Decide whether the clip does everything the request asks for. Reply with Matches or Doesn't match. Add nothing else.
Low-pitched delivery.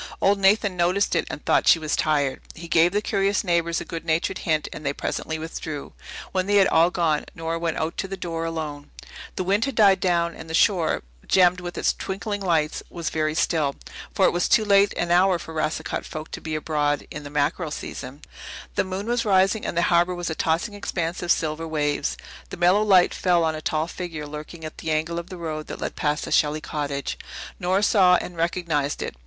Doesn't match